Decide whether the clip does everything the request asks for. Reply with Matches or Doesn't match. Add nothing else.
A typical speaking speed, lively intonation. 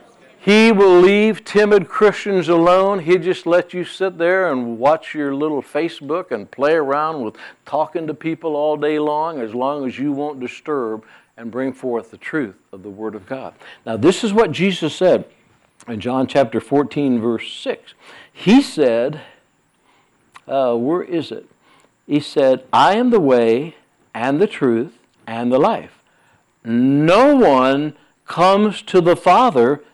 Matches